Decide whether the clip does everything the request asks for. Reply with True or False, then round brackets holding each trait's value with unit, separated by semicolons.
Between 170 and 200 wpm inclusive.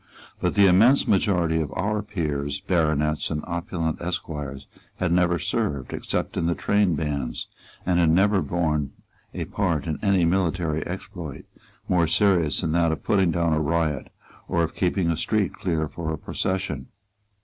False (160 wpm)